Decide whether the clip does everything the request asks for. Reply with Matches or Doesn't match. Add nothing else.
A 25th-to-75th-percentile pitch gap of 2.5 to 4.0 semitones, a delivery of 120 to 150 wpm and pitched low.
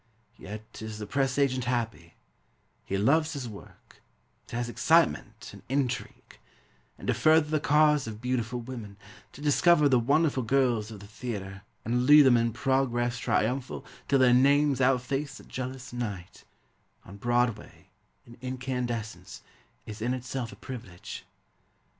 Matches